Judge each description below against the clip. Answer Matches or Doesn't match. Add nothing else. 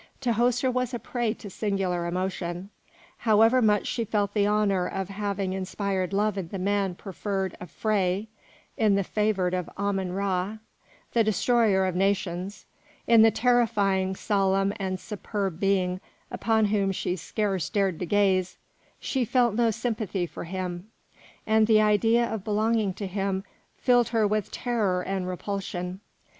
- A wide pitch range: Doesn't match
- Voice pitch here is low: Doesn't match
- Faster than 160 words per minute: Doesn't match